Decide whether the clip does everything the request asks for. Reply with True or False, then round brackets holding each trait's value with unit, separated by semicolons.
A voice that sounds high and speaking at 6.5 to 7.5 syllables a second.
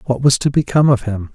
False (125 Hz; 6.8 syllables/s)